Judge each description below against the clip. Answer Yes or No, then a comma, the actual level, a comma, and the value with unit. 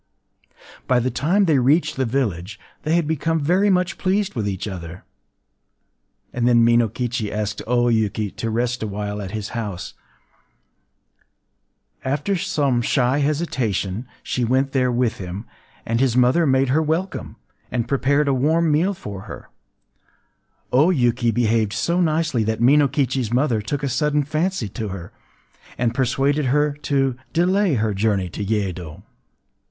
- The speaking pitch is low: Yes, low, 125 Hz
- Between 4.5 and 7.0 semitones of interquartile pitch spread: Yes, average, 5.3 semitones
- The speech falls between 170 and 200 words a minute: No, average, 150 wpm